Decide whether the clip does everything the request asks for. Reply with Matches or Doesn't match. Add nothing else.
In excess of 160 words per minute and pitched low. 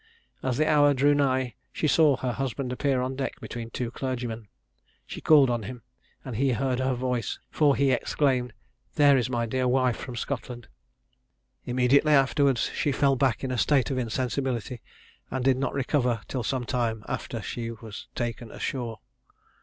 Matches